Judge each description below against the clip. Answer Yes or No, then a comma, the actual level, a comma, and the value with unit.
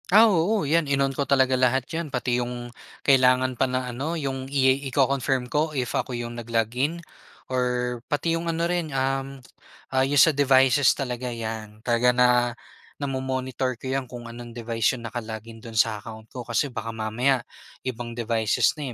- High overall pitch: No, low, 130 Hz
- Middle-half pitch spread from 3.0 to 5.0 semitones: No, narrow, 2.6 semitones